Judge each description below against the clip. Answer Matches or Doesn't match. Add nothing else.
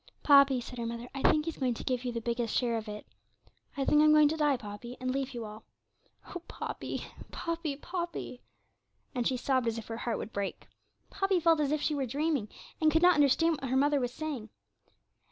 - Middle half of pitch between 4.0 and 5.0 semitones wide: Matches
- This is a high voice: Matches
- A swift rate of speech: Matches